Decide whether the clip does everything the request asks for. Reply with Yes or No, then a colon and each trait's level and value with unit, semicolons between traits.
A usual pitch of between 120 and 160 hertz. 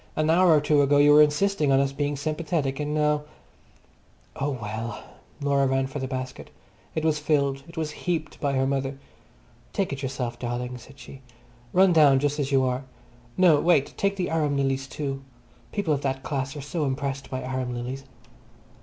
Yes: medium, 140 Hz